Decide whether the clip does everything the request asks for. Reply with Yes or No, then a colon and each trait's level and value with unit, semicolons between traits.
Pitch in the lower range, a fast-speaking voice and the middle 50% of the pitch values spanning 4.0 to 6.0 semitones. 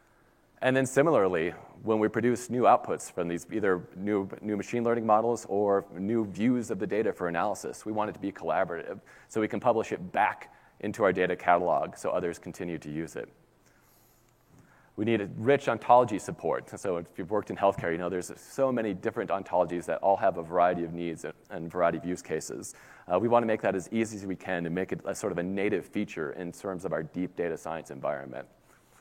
Yes: low, 100 Hz; fast, 215 wpm; average, 4.5 semitones